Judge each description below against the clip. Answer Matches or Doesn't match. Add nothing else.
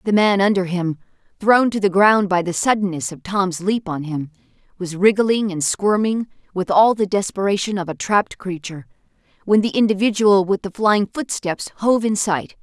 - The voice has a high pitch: Matches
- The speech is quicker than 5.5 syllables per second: Doesn't match